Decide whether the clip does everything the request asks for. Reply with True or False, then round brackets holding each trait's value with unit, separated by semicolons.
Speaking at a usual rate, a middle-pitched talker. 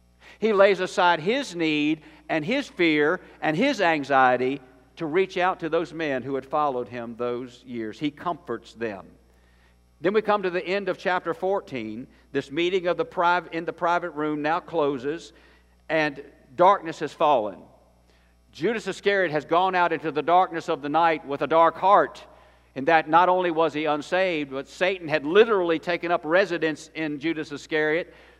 True (175 wpm; 160 Hz)